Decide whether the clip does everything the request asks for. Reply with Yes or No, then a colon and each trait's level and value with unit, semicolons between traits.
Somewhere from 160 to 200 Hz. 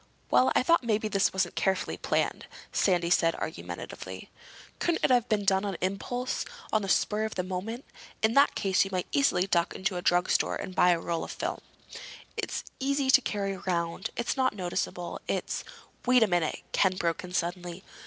Yes: high, 190 Hz